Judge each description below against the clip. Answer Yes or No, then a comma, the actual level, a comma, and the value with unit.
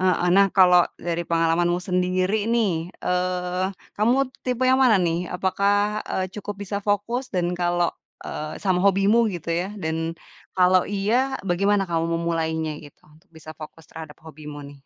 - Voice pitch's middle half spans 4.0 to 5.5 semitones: No, average, 3.5 semitones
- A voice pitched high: No, medium, 180 Hz